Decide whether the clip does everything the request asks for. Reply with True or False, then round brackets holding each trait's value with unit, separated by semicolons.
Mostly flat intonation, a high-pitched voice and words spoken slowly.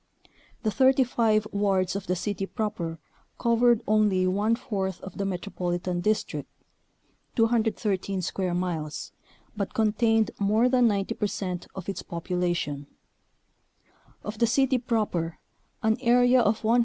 False (3.7 semitones; 205 Hz; 125 wpm)